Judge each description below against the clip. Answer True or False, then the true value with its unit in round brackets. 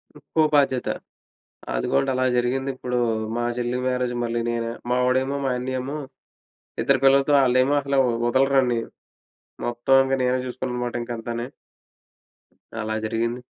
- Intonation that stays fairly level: True (1.8 semitones)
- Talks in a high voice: False (125 Hz)